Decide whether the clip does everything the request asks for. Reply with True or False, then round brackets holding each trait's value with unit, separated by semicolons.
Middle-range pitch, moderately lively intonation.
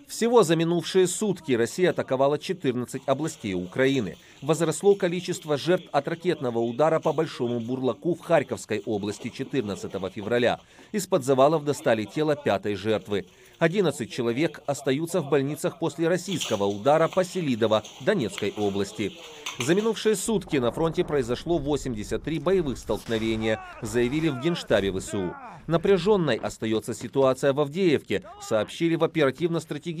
False (145 Hz; 6.3 semitones)